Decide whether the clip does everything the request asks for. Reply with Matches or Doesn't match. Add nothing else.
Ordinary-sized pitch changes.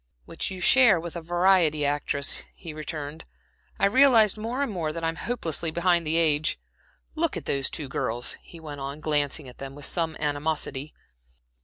Matches